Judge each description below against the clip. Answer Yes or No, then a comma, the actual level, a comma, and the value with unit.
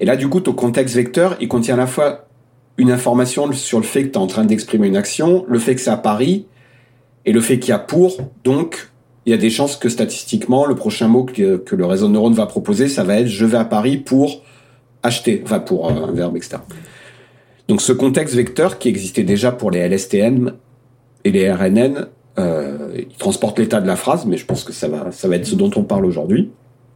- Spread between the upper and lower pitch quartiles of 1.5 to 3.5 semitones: No, average, 4.0 semitones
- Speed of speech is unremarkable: No, fast, 235 wpm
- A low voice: Yes, low, 125 Hz